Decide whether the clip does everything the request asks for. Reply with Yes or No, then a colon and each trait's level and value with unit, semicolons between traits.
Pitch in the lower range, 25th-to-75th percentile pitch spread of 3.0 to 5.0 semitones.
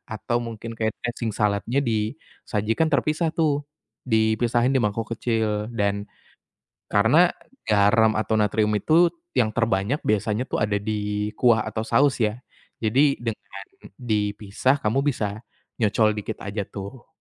No: low, 110 Hz; narrow, 2.6 semitones